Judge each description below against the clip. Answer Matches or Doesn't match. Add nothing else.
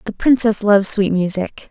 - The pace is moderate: Matches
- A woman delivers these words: Matches